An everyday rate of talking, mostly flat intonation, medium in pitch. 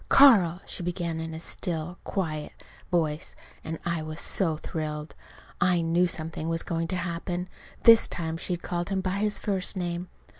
Yes: average, 165 wpm; narrow, 2.0 semitones; medium, 170 Hz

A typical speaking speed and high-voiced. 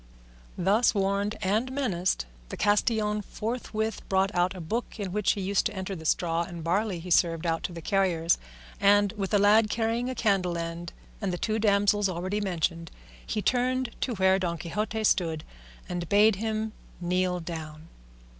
Yes: average, 175 wpm; high, 195 Hz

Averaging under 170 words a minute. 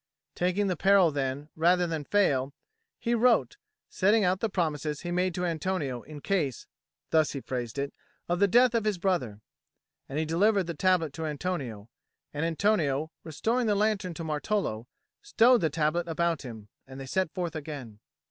No: average, 175 wpm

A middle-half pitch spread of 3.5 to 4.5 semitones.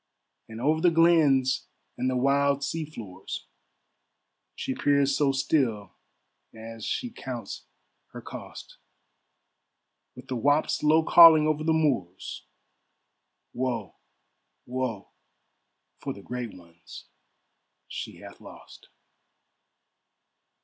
No: average, 4.9 semitones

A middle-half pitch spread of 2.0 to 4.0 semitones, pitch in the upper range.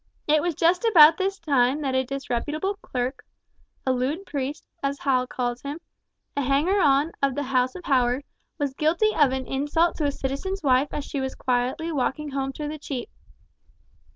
Yes: average, 2.9 semitones; very high, 280 Hz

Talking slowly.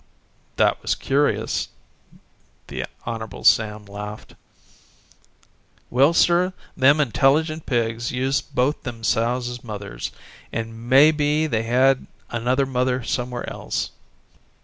Yes: slow, 110 wpm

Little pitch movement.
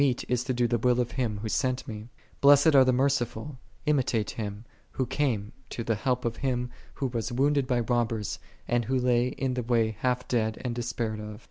Yes: narrow, 2.2 semitones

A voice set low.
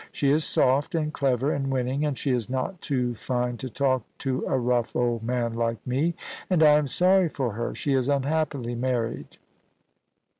Yes: low, 130 Hz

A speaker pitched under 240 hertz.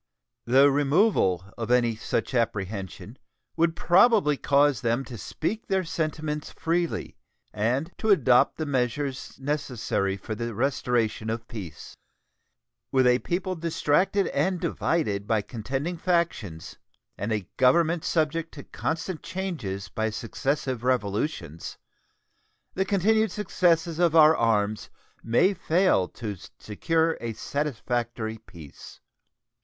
Yes: low, 135 Hz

